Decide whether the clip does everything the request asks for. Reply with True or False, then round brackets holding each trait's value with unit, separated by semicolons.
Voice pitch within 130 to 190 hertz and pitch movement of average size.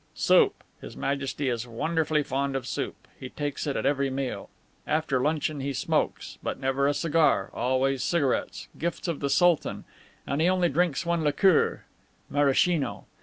True (140 Hz; 3.2 semitones)